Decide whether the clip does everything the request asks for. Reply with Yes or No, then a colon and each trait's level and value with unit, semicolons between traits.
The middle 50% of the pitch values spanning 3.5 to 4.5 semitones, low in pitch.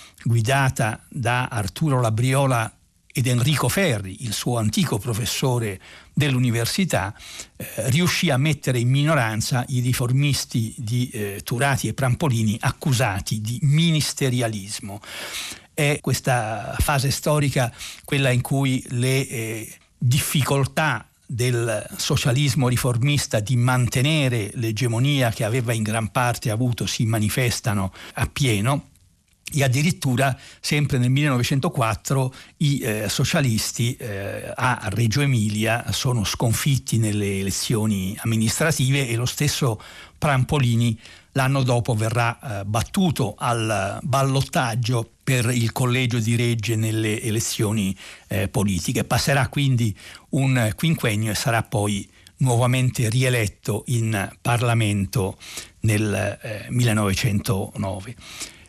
Yes: average, 3.8 semitones; low, 120 Hz